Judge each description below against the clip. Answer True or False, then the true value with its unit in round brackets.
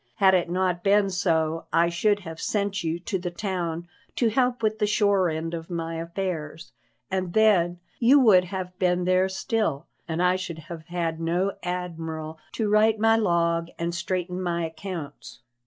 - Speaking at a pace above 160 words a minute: True (170 wpm)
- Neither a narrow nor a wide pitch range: True (3.0 semitones)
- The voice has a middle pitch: True (180 Hz)